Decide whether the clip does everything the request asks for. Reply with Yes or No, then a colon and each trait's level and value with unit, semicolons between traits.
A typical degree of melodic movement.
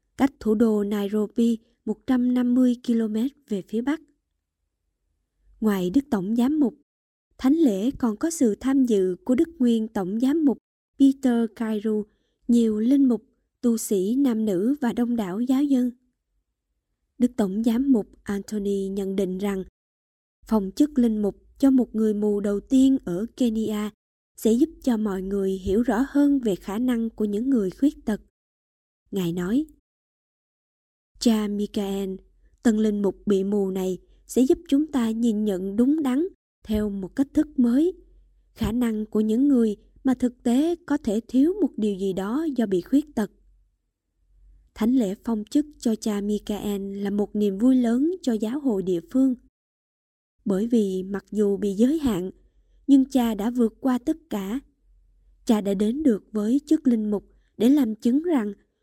Yes: average, 4.3 semitones